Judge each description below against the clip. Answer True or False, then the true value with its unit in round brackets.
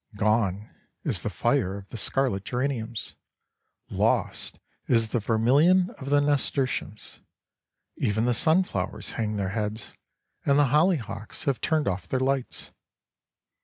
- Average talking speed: False (130 wpm)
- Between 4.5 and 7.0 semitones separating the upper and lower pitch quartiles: True (4.9 semitones)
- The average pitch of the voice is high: False (120 Hz)